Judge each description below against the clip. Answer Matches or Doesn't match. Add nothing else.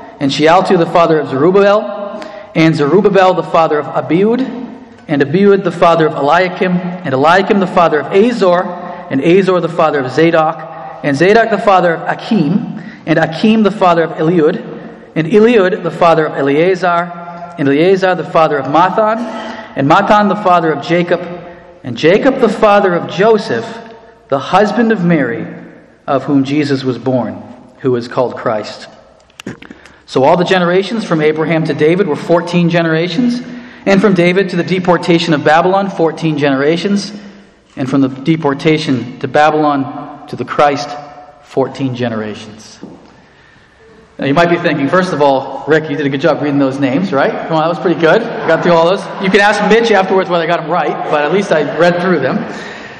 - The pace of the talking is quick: Doesn't match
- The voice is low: Doesn't match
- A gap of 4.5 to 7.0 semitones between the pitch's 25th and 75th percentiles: Matches